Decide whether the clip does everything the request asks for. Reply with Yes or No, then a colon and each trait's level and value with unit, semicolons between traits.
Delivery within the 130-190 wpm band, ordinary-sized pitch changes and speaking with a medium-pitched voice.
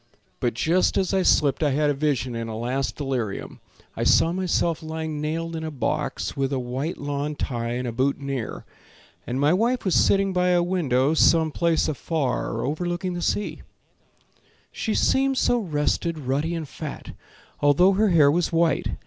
Yes: average, 175 wpm; average, 4.2 semitones; medium, 155 Hz